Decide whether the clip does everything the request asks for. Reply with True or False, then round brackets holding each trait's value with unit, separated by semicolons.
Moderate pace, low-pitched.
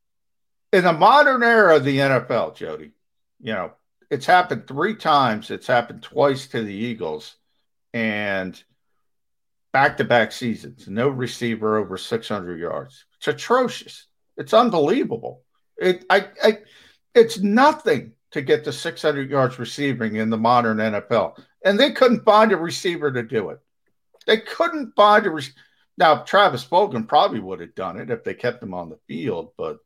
False (155 wpm; 145 Hz)